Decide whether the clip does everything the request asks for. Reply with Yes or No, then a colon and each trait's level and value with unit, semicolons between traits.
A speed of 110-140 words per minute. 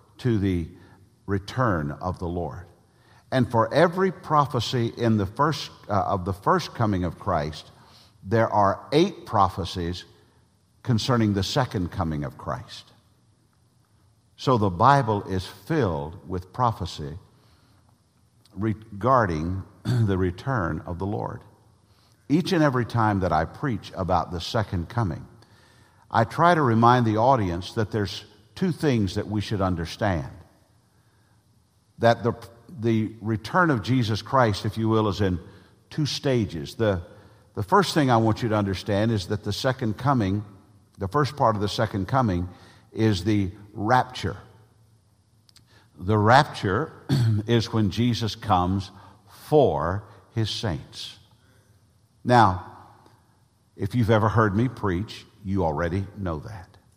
Yes: slow, 135 wpm